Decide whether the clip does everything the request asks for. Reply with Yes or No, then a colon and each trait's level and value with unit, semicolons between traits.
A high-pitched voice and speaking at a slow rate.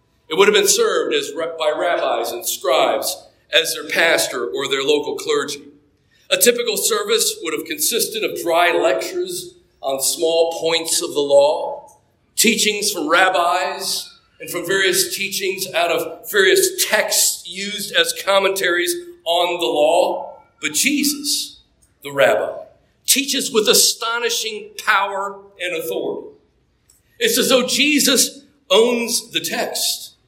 Yes: very high, 270 Hz; slow, 130 wpm